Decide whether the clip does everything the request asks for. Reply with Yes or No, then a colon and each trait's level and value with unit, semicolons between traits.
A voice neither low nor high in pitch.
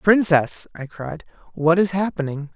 Yes: medium, 165 Hz